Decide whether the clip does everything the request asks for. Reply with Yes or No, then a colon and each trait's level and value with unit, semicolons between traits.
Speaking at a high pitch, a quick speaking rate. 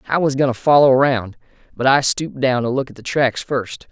No: low, 130 Hz; fast, 245 wpm